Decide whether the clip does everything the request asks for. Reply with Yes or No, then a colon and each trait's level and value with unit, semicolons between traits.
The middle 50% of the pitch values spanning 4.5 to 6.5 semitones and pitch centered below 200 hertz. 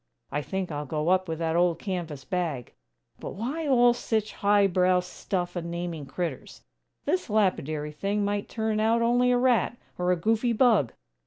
Yes: average, 4.8 semitones; medium, 185 Hz